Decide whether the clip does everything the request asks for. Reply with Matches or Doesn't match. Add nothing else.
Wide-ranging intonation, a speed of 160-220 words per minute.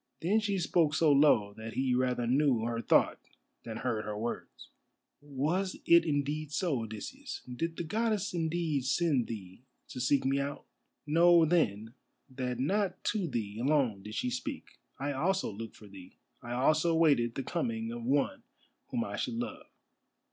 Matches